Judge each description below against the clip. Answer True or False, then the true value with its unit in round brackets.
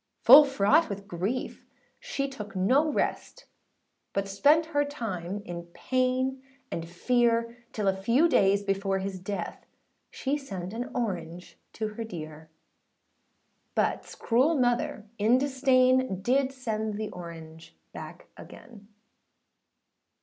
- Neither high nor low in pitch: False (220 Hz)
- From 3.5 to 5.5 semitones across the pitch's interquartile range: True (5.2 semitones)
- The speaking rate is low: True (125 wpm)